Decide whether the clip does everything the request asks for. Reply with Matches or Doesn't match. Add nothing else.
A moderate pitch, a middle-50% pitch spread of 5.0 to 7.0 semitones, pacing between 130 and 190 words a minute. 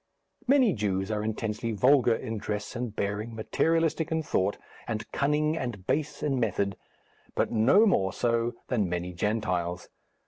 Doesn't match